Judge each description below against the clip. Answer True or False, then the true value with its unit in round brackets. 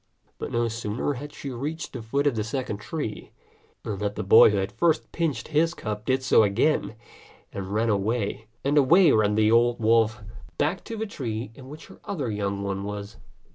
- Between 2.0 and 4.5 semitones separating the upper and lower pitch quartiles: False (5.3 semitones)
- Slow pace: False (180 wpm)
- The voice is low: True (115 Hz)